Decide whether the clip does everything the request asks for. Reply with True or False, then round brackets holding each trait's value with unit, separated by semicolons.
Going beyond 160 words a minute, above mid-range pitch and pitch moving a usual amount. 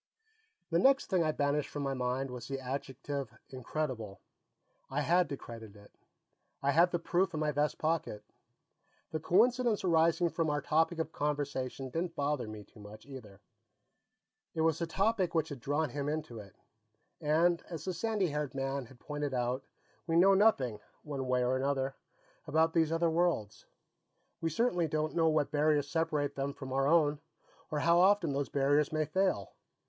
False (175 wpm; 150 Hz; 3.6 semitones)